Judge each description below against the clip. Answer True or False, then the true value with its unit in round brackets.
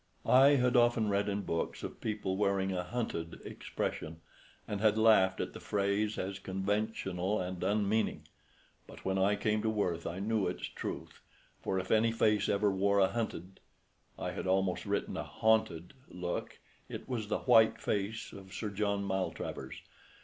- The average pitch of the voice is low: True (100 Hz)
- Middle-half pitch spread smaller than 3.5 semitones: True (2.5 semitones)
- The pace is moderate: True (165 wpm)